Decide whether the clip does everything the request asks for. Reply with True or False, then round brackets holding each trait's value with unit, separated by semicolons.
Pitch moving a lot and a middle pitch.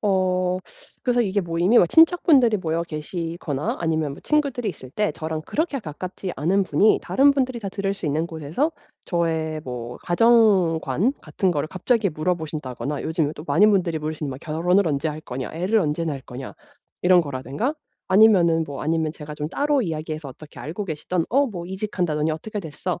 False (4.8 semitones; 170 Hz)